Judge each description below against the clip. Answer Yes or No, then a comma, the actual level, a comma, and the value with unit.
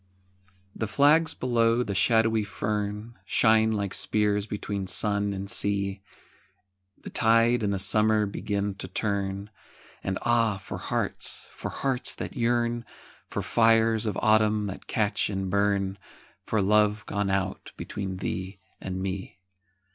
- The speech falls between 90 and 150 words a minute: Yes, slow, 135 wpm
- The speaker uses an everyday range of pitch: No, narrow, 2.2 semitones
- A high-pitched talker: No, low, 105 Hz